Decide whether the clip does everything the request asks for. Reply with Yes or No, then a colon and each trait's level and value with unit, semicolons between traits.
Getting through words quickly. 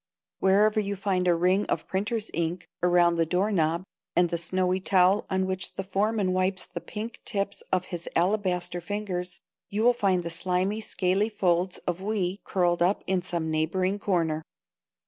No: average, 170 wpm